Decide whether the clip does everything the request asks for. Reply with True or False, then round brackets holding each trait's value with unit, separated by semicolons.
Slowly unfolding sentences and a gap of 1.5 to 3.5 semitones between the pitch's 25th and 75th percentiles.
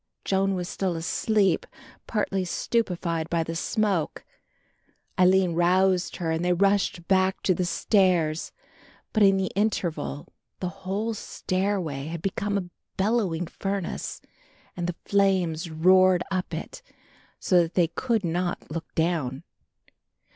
True (130 wpm; 2.5 semitones)